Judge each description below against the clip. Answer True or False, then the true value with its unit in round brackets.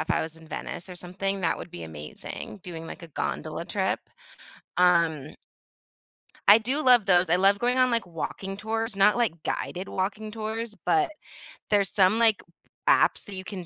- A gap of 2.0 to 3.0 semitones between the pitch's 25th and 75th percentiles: False (3.9 semitones)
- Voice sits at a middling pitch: False (195 Hz)